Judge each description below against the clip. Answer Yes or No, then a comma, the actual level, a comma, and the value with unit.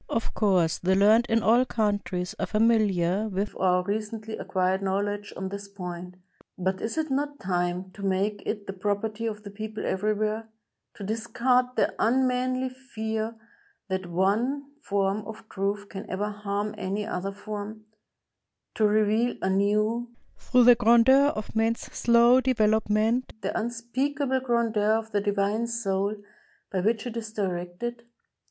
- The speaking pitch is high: Yes, high, 215 Hz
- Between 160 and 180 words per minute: No, average, 150 wpm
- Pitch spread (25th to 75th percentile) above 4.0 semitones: No, average, 2.8 semitones